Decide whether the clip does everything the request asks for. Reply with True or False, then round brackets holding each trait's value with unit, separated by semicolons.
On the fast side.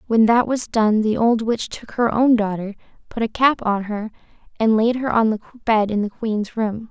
True (225 wpm)